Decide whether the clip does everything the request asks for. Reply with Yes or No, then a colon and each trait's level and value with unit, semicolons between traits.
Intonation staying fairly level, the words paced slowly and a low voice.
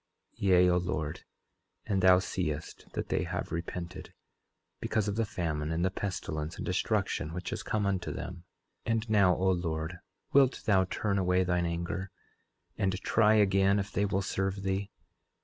No: narrow, 2.2 semitones; average, 170 wpm; very low, 95 Hz